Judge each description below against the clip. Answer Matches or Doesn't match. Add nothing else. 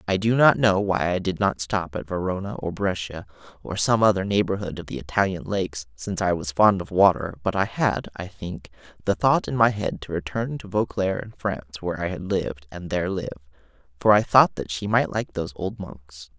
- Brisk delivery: Matches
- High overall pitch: Doesn't match